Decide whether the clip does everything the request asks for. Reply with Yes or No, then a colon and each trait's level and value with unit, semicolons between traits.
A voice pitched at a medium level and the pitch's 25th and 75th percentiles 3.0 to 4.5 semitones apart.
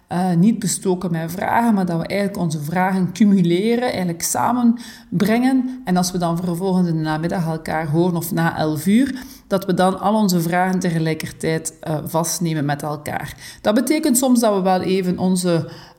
Yes: medium, 180 Hz; average, 3.5 semitones